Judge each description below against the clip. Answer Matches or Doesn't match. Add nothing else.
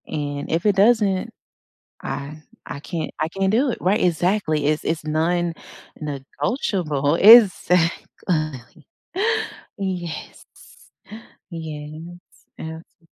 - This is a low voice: Doesn't match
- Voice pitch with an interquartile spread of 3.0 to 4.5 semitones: Matches